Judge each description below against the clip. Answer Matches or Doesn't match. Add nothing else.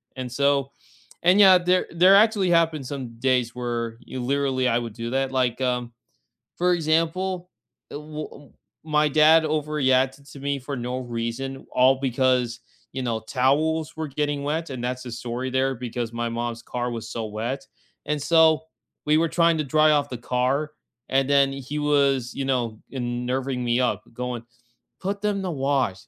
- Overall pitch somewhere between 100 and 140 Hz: Matches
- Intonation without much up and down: Doesn't match